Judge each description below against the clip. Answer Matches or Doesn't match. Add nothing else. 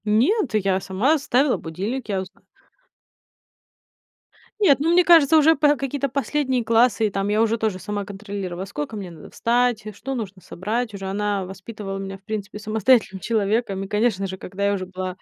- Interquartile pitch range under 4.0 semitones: Doesn't match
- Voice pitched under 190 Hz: Doesn't match